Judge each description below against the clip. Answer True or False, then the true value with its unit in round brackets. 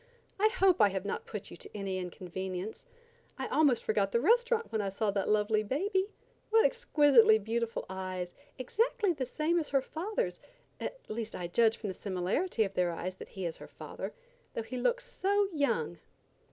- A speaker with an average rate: True (185 wpm)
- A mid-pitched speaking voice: False (225 Hz)